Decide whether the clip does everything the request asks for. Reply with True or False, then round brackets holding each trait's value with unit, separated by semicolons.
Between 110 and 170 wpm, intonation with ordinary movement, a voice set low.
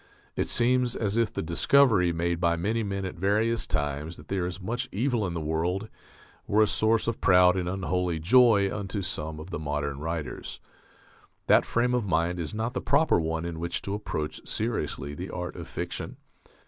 False (190 wpm; 5.0 semitones; 95 Hz)